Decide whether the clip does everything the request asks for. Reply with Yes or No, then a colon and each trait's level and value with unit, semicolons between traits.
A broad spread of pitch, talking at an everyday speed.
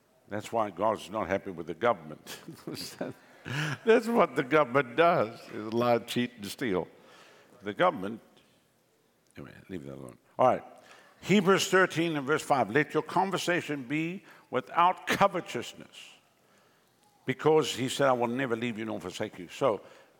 Yes: wide, 7.5 semitones; average, 145 wpm